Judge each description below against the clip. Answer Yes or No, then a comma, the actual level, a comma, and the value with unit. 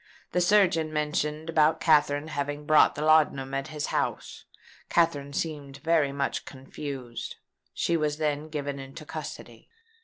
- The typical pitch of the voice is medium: Yes, medium, 150 Hz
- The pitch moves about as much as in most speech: No, narrow, 1.8 semitones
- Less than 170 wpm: Yes, average, 140 wpm